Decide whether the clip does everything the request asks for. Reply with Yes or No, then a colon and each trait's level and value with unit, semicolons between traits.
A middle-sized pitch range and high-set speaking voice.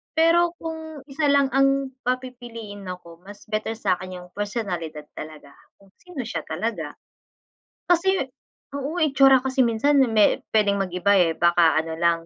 No: wide, 7.2 semitones; high, 225 Hz